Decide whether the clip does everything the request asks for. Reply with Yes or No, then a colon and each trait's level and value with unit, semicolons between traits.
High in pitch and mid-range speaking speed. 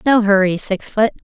Yes: high, 210 Hz; average, 180 wpm